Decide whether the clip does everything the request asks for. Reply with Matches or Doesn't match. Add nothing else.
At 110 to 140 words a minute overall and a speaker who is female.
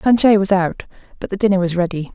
Doesn't match